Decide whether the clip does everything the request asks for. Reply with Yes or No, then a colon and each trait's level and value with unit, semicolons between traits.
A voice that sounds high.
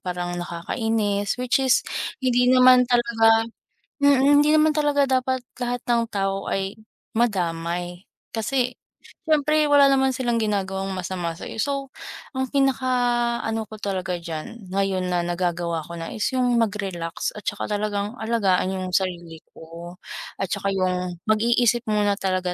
Yes: high, 210 Hz